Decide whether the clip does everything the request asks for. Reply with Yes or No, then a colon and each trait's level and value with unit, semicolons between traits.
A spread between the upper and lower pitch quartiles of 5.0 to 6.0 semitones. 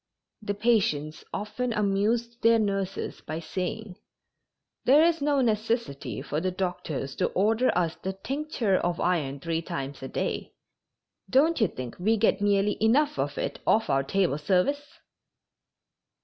Yes: wide, 5.5 semitones